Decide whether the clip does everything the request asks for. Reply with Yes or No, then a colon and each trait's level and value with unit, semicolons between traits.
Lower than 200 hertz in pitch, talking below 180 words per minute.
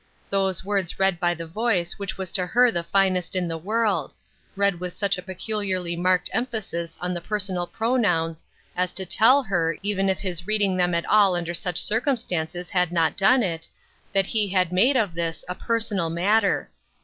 No: medium, 185 Hz; average, 190 wpm